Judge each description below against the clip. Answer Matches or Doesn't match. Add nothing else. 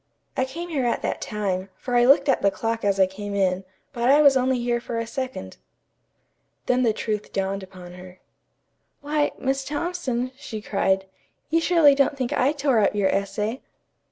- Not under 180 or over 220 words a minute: Matches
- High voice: Matches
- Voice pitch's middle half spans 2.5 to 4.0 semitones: Doesn't match